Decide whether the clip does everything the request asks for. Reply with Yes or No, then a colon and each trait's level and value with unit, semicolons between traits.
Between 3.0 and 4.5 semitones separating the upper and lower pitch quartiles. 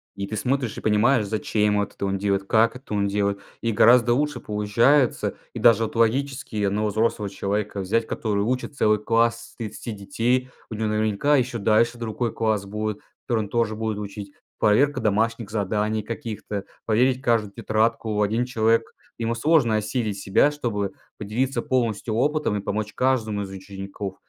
No: narrow, 2.4 semitones